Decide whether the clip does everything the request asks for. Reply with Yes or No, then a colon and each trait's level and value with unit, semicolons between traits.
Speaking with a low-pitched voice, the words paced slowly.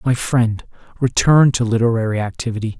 Yes: low, 115 Hz; slow, 130 wpm